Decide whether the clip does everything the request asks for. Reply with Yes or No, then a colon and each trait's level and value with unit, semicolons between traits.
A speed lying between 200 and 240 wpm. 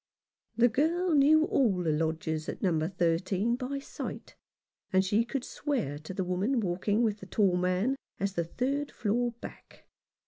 No: average, 165 wpm